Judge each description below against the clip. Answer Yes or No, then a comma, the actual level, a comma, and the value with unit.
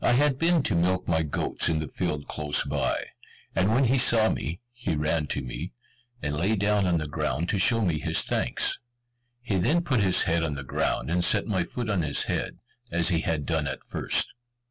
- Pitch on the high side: No, very low, 85 Hz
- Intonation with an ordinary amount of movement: No, wide, 6.0 semitones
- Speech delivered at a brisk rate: Yes, fast, 215 wpm